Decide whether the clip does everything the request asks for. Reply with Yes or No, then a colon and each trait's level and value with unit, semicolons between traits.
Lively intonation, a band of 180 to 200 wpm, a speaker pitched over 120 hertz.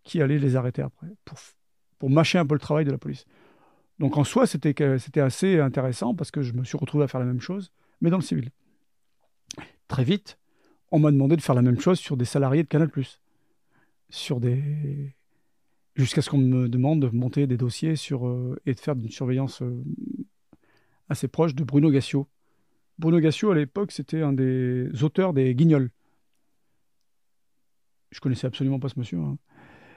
No: average, 3.3 semitones; average, 185 wpm; medium, 140 Hz